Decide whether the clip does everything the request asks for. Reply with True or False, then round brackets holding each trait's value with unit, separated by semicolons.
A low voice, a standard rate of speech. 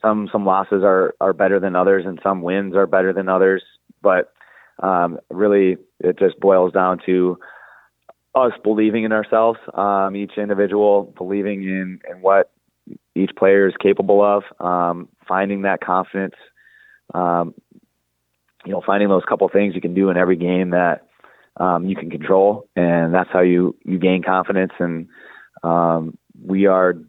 True (95 Hz; 160 wpm)